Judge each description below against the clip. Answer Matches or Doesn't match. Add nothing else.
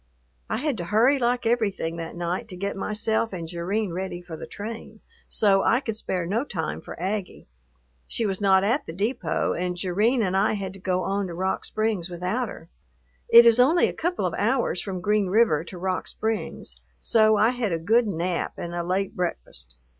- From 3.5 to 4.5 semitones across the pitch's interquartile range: Matches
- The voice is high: Matches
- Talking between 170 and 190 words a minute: Doesn't match